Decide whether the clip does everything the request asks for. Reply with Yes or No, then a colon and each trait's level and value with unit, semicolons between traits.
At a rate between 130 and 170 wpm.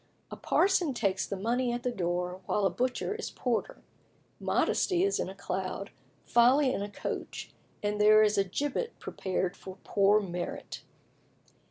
Yes: average, 160 wpm